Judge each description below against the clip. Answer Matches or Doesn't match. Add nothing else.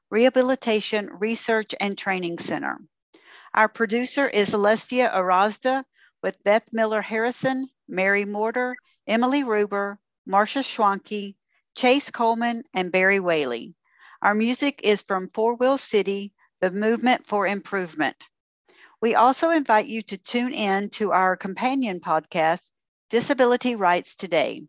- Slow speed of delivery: Matches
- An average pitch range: Matches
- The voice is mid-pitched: Doesn't match